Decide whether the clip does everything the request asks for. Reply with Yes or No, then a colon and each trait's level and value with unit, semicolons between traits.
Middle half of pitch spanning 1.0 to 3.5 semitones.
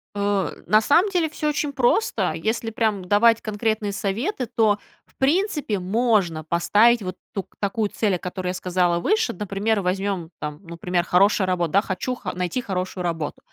No: average, 4.2 semitones